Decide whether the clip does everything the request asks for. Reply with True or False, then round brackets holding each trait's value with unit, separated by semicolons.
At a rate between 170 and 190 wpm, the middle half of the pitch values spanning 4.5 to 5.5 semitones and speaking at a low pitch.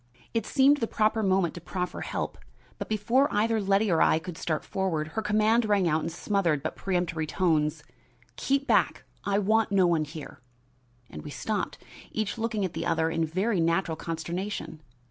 False (180 wpm; 4.8 semitones; 190 Hz)